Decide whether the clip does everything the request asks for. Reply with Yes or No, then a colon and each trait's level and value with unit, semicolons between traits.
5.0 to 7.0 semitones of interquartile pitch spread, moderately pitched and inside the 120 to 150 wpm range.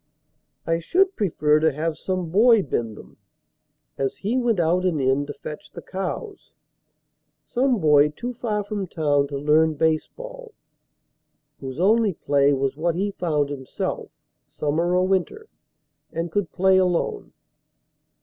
Yes: wide, 5.5 semitones; medium, 170 Hz; average, 140 wpm